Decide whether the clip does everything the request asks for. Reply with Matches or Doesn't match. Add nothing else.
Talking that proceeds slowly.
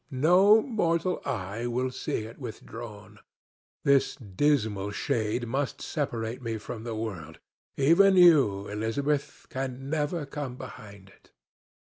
Matches